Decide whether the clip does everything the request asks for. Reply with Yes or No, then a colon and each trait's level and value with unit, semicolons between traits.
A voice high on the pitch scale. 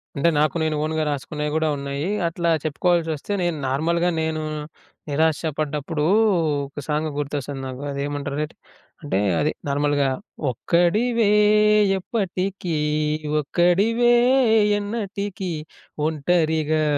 No: medium, 155 Hz